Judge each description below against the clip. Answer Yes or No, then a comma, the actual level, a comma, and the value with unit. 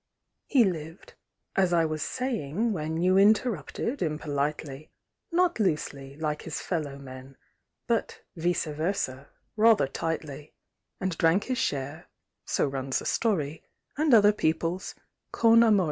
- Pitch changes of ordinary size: No, wide, 6.0 semitones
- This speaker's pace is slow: Yes, slow, 130 wpm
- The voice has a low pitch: No, medium, 165 Hz